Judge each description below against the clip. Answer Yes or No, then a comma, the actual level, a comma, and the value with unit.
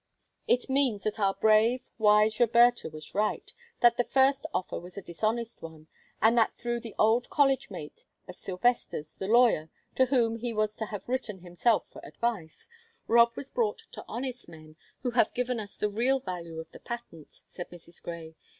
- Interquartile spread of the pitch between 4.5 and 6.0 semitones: Yes, average, 4.9 semitones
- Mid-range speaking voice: No, high, 220 Hz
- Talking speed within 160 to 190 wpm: Yes, average, 185 wpm